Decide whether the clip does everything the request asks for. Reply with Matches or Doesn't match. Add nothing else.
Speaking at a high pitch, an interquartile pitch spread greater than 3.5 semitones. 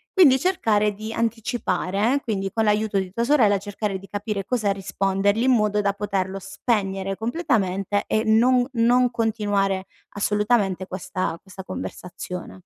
Doesn't match